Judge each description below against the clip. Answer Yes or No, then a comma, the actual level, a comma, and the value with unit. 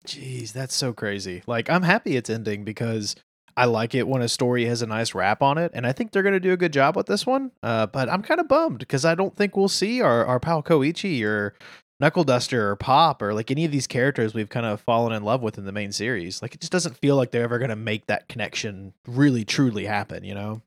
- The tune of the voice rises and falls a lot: Yes, wide, 7.0 semitones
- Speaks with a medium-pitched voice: No, low, 125 Hz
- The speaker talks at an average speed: No, fast, 260 wpm